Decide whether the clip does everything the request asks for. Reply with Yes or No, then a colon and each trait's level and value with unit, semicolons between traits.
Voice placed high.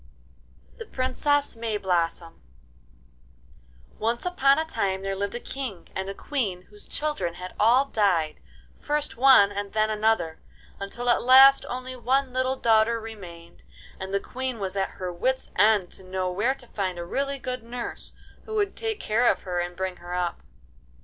Yes: high, 220 Hz